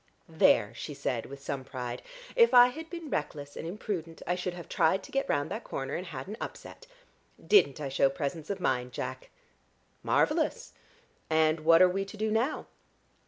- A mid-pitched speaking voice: Yes, medium, 165 Hz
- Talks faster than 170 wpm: Yes, average, 185 wpm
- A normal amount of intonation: No, wide, 7.1 semitones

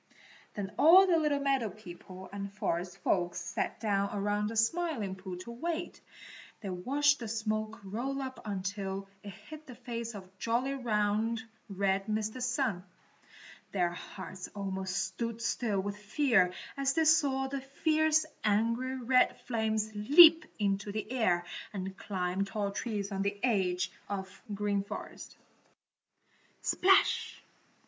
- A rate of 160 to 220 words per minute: No, average, 140 wpm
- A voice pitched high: Yes, high, 215 Hz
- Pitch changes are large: No, average, 4.7 semitones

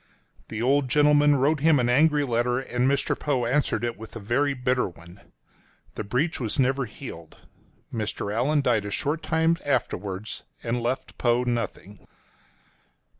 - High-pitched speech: No, low, 125 Hz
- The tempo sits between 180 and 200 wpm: No, average, 155 wpm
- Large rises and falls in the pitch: No, average, 4.0 semitones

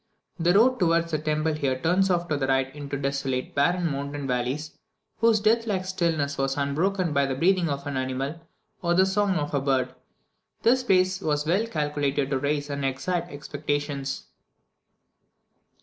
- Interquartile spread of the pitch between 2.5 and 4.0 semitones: No, average, 4.5 semitones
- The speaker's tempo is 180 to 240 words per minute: No, average, 165 wpm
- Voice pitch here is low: No, medium, 150 Hz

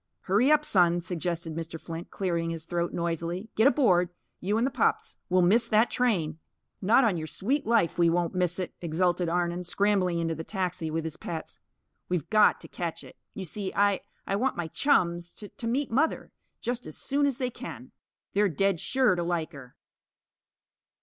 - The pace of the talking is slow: No, average, 190 wpm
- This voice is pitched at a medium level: Yes, medium, 180 Hz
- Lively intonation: No, average, 4.4 semitones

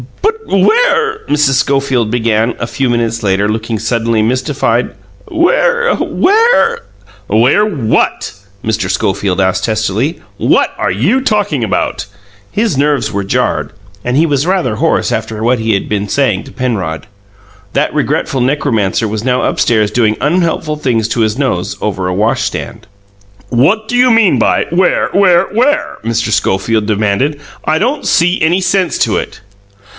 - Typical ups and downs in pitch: No, wide, 8.4 semitones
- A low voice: Yes, low, 125 Hz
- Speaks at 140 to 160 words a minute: Yes, average, 150 wpm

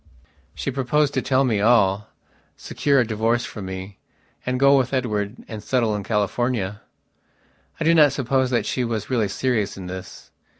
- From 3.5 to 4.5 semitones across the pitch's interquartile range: Yes, average, 4.0 semitones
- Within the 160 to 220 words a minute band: Yes, average, 170 wpm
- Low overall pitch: Yes, low, 120 Hz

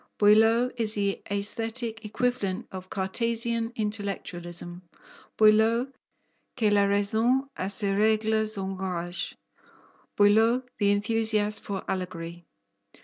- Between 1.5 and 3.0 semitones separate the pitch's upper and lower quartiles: Yes, narrow, 2.4 semitones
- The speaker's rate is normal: No, slow, 95 wpm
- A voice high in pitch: Yes, high, 210 Hz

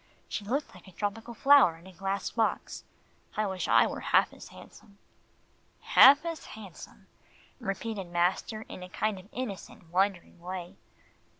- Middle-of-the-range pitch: No, high, 200 Hz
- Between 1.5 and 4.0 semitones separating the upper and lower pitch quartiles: Yes, average, 3.3 semitones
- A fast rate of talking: No, average, 155 wpm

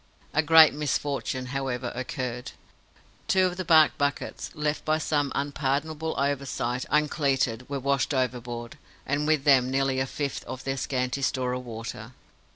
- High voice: No, low, 135 Hz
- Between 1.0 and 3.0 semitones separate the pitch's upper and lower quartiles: Yes, average, 2.7 semitones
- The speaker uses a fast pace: No, average, 150 wpm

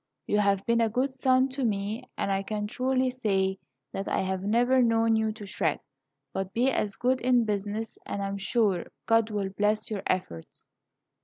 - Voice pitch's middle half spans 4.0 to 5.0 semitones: No, average, 3.5 semitones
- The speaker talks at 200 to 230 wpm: No, average, 185 wpm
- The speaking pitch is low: No, high, 215 Hz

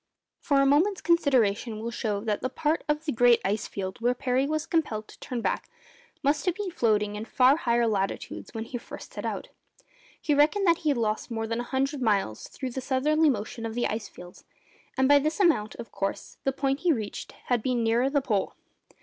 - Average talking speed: No, fast, 215 wpm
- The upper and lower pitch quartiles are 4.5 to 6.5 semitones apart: Yes, average, 4.8 semitones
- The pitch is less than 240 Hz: No, very high, 250 Hz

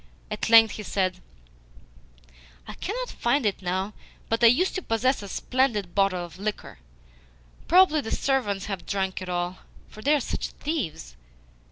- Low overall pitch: No, high, 210 Hz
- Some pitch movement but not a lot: No, wide, 5.9 semitones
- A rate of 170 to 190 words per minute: No, average, 160 wpm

